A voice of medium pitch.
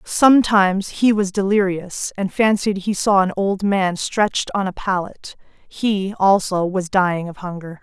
No: high, 195 Hz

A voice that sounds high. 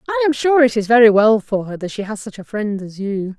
Yes: high, 225 Hz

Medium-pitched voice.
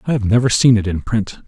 No: low, 110 Hz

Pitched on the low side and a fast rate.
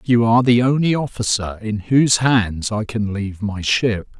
No: low, 115 Hz; average, 185 wpm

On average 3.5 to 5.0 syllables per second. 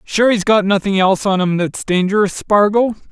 No: 5.2 syllables/s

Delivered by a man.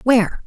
No: female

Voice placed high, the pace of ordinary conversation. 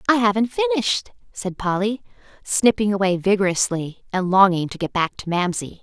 Yes: high, 200 Hz; average, 155 wpm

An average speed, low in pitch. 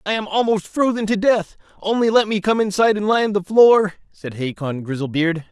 No: average, 195 wpm; high, 200 Hz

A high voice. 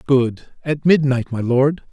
No: low, 135 Hz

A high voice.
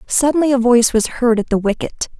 Yes: high, 245 Hz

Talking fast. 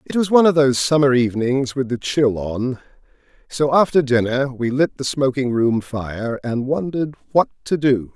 No: average, 185 wpm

